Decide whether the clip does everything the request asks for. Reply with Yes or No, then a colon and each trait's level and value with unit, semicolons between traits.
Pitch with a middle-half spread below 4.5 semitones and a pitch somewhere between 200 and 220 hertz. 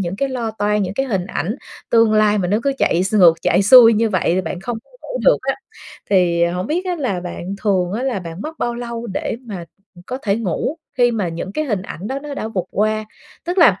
No: average, 4.8 semitones; high, 215 Hz